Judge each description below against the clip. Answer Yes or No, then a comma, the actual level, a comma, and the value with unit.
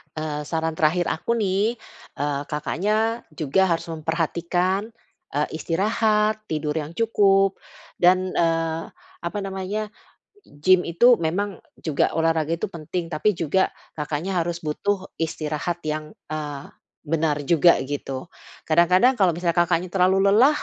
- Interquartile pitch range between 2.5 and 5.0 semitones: Yes, average, 3.7 semitones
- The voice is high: No, medium, 170 Hz